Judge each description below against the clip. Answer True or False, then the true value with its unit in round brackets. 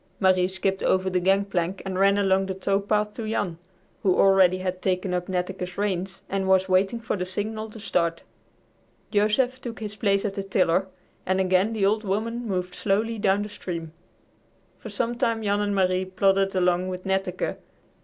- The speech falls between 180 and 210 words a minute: True (185 wpm)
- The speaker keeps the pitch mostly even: True (1.9 semitones)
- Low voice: False (195 Hz)